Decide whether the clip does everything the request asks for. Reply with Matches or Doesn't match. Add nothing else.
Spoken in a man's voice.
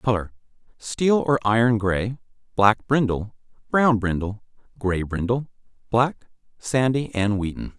Matches